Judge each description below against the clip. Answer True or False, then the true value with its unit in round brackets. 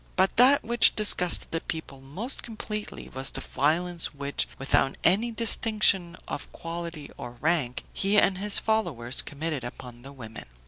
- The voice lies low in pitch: False (170 Hz)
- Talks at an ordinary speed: True (150 wpm)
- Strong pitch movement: True (7.3 semitones)